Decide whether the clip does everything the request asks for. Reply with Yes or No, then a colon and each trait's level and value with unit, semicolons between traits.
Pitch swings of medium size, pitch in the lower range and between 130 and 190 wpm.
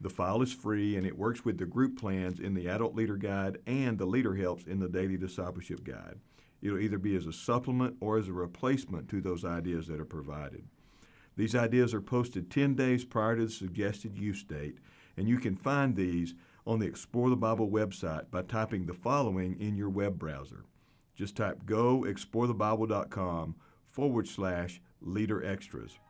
Yes: average, 4.0 semitones; low, 100 Hz; average, 185 wpm